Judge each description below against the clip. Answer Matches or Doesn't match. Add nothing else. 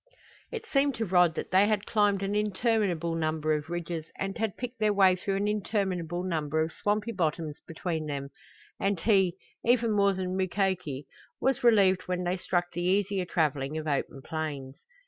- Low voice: Doesn't match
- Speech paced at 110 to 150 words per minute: Doesn't match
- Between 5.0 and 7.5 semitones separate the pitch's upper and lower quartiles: Doesn't match